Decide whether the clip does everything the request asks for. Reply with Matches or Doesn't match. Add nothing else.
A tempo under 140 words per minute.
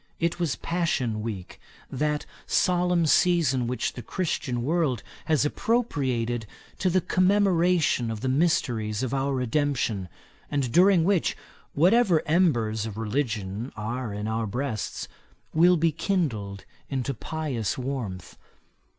Matches